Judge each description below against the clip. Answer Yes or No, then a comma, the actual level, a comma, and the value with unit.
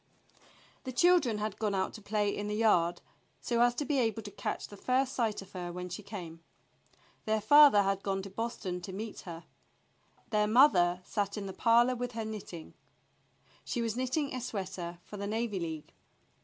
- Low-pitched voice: No, high, 210 Hz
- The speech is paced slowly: No, average, 190 wpm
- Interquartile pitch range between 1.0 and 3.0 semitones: No, average, 3.7 semitones